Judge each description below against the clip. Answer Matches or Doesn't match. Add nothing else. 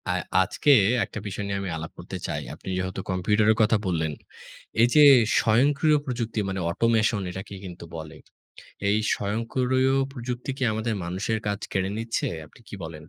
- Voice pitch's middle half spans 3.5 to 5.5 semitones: Matches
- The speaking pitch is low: Matches